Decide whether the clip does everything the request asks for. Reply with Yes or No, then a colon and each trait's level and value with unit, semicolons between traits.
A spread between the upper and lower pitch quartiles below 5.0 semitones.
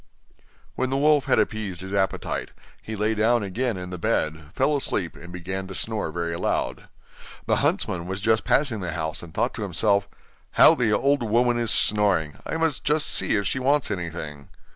No: average, 5.3 semitones